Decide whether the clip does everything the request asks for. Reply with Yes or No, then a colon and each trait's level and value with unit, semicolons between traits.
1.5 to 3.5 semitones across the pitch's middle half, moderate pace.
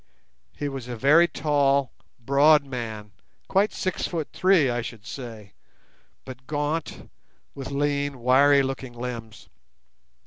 No: average, 3.2 semitones; slow, 125 wpm